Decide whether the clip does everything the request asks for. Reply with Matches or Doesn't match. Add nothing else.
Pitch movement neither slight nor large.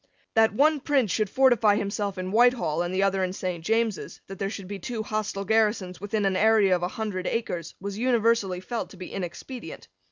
Matches